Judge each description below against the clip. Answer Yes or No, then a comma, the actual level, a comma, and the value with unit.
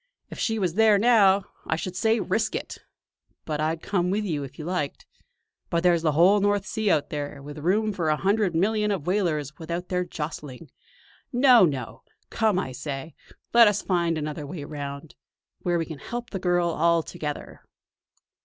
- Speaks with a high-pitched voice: No, medium, 175 Hz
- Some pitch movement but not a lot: Yes, average, 5.0 semitones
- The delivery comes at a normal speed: Yes, average, 180 wpm